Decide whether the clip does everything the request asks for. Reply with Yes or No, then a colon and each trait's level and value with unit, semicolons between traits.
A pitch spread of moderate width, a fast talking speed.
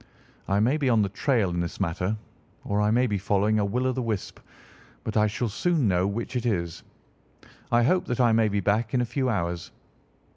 Yes: average, 3.6 semitones; fast, 220 wpm